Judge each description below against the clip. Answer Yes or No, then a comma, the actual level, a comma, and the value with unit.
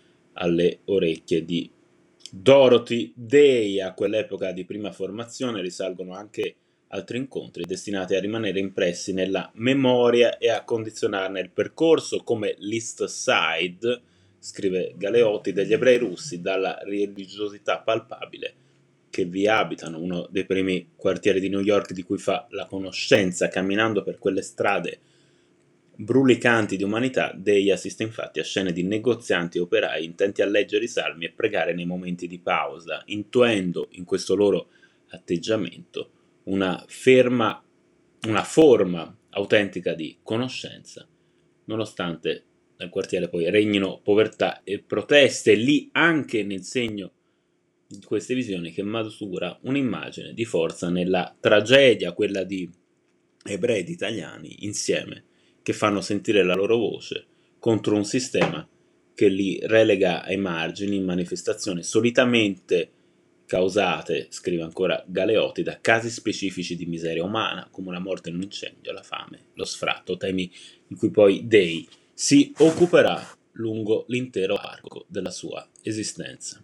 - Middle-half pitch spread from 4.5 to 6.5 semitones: No, average, 4.0 semitones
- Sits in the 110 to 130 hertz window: No, low, 100 Hz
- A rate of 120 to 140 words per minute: Yes, average, 130 wpm